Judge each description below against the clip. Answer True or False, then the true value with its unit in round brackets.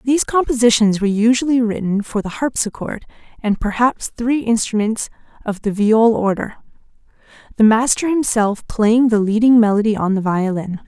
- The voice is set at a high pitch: True (225 Hz)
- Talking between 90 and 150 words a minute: True (145 wpm)